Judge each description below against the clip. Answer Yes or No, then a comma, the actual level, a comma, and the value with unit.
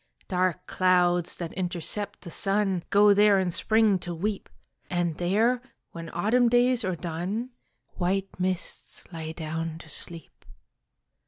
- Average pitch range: Yes, average, 3.1 semitones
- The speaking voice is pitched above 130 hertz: Yes, medium, 185 Hz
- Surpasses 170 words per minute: No, slow, 135 wpm